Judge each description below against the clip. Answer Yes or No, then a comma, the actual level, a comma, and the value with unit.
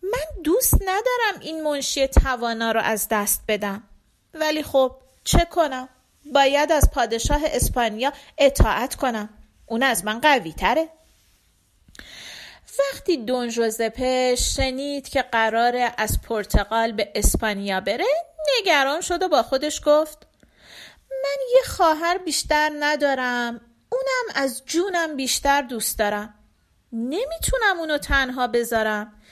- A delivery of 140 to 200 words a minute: No, average, 115 wpm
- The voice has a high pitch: Yes, very high, 275 Hz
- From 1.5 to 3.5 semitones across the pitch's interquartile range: No, wide, 5.4 semitones